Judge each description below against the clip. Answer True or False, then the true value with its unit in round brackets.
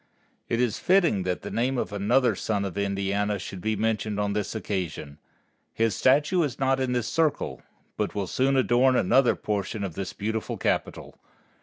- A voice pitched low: True (110 Hz)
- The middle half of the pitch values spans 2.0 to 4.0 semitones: False (4.5 semitones)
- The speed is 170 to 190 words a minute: True (175 wpm)